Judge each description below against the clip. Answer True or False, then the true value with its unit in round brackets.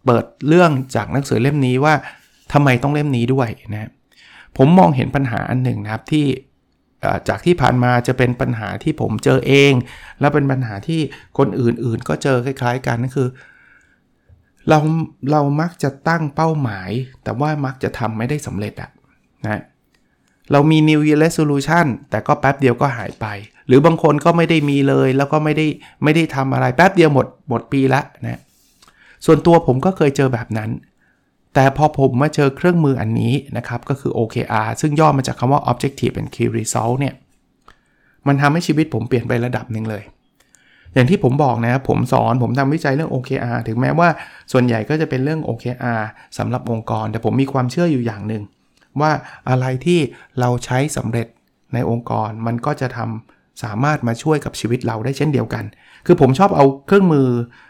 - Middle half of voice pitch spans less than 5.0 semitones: True (3.9 semitones)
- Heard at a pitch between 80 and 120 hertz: False (130 Hz)